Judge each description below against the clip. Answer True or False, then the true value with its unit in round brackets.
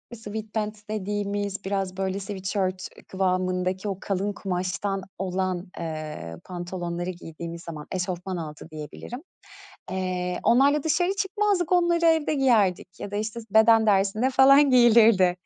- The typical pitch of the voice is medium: False (195 Hz)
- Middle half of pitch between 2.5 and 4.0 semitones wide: True (3.7 semitones)